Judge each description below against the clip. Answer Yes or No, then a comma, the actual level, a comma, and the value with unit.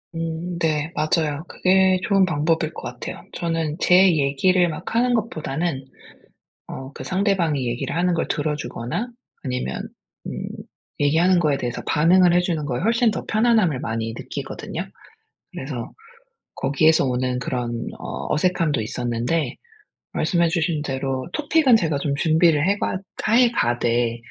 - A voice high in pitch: No, medium, 160 Hz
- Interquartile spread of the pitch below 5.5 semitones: Yes, average, 5.1 semitones